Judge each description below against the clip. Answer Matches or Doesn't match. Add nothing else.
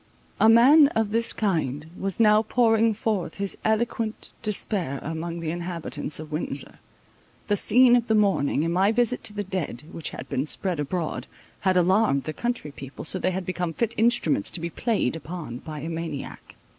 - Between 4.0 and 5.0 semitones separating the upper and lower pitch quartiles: Doesn't match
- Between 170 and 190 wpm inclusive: Matches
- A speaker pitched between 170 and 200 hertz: Matches